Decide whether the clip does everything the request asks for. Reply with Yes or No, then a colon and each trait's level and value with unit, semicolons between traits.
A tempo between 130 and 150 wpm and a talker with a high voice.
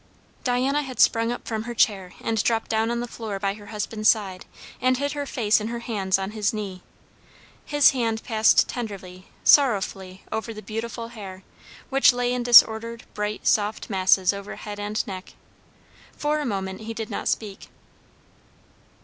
No: average, 170 wpm; high, 220 Hz